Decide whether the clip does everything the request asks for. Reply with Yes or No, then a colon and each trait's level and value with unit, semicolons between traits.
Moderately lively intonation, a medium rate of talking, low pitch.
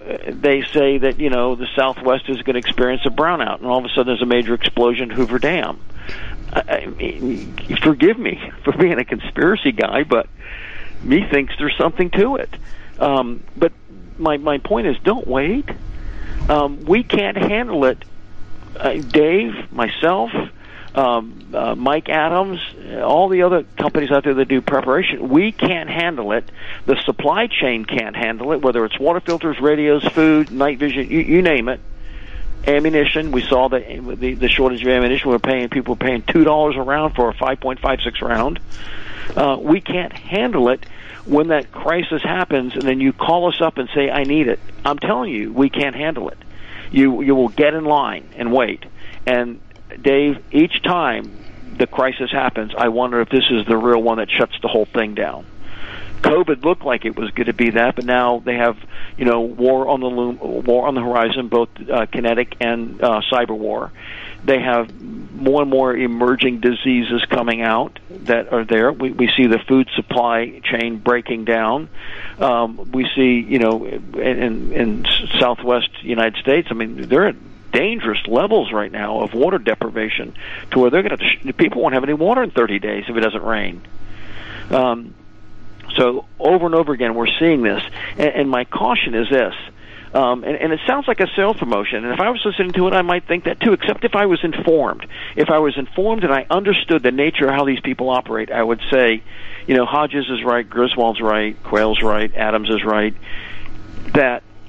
Yes: average, 4.3 semitones; average, 190 wpm; low, 125 Hz